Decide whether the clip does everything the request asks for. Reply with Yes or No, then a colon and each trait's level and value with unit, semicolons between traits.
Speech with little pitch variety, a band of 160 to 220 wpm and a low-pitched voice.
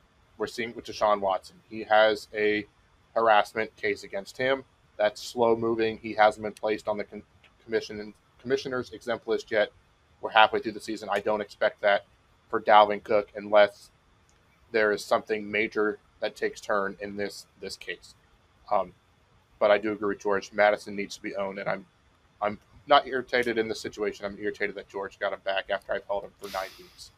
Yes: narrow, 1.4 semitones; average, 190 wpm; low, 105 Hz